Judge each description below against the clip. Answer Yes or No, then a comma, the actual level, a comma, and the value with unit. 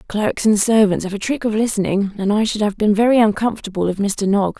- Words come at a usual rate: No, fast, 235 wpm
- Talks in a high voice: Yes, high, 210 Hz